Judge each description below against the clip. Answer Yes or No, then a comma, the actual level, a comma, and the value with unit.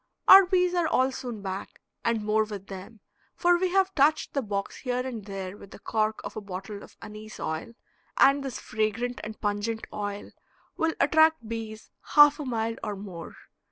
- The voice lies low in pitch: No, high, 220 Hz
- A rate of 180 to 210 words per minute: Yes, average, 185 wpm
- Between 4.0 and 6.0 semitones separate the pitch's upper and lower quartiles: Yes, average, 5.1 semitones